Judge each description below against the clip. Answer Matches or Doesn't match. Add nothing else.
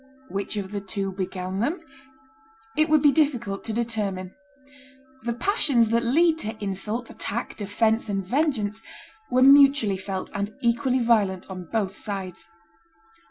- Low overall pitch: Doesn't match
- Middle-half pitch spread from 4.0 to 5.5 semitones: Matches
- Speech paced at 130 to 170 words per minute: Matches